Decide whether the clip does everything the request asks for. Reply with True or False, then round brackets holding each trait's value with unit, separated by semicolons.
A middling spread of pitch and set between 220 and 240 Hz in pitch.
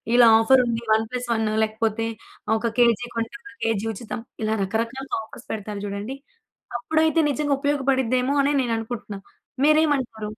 True (3.4 semitones; 235 Hz)